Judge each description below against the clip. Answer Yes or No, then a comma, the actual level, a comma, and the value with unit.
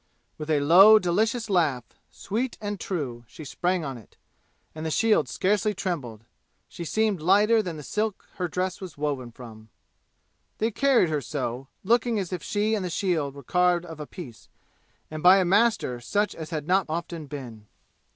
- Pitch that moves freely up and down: Yes, wide, 5.9 semitones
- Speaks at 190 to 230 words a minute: No, average, 180 wpm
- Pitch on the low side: No, medium, 175 Hz